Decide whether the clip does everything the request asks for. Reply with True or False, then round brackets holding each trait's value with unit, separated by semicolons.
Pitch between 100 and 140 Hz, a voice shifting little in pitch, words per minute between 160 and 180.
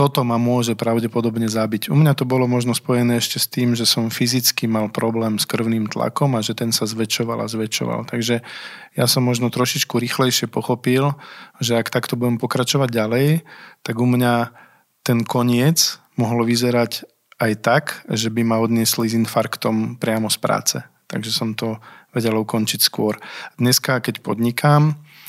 True (120 Hz; 1.9 semitones; 165 wpm)